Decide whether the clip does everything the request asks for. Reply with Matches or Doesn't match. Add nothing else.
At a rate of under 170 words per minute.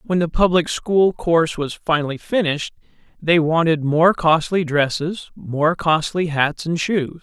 Matches